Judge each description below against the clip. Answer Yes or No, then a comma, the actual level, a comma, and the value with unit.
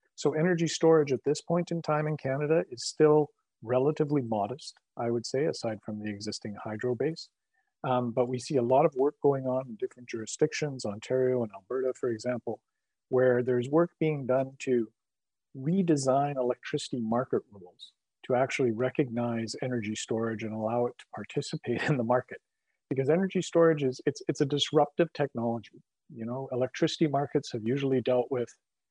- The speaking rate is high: No, average, 170 wpm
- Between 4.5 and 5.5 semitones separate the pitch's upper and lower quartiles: No, average, 4.1 semitones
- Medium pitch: No, low, 130 Hz